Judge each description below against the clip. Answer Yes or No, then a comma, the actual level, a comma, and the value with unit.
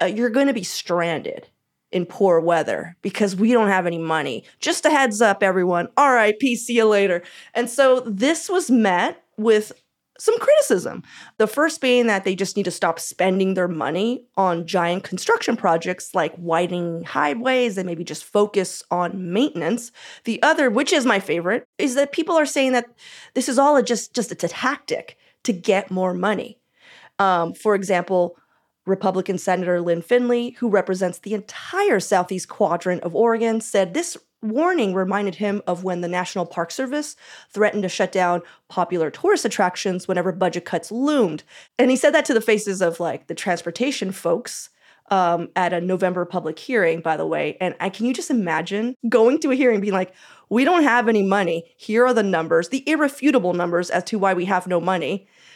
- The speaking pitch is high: Yes, high, 200 Hz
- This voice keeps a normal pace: Yes, average, 185 wpm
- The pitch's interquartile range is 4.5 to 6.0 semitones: Yes, wide, 5.6 semitones